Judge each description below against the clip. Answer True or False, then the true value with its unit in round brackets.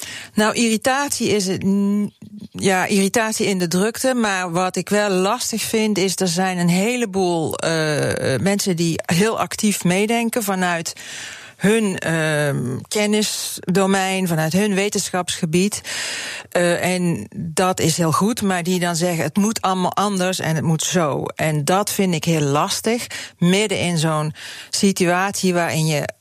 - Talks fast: False (145 wpm)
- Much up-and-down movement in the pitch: False (2.9 semitones)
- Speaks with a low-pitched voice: False (185 Hz)